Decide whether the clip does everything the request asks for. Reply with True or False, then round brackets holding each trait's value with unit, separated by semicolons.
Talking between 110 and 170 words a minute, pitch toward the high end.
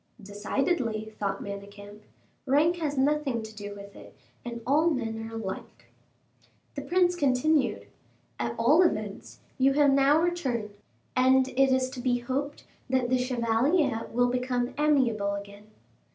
True (140 wpm; 250 Hz)